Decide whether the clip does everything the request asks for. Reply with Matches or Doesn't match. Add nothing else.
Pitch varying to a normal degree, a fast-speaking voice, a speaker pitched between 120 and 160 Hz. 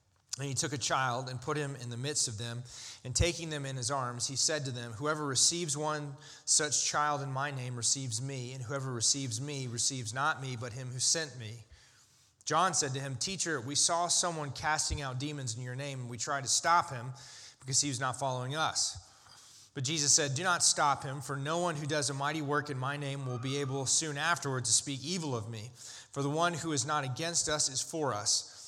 Matches